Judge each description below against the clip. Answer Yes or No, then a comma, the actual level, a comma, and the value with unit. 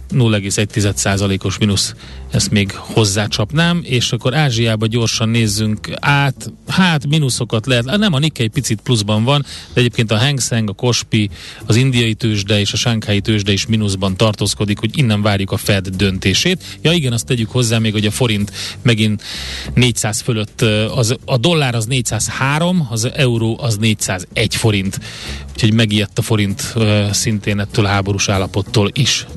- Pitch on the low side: Yes, low, 110 Hz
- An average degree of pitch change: Yes, average, 3.1 semitones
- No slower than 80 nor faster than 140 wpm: No, fast, 155 wpm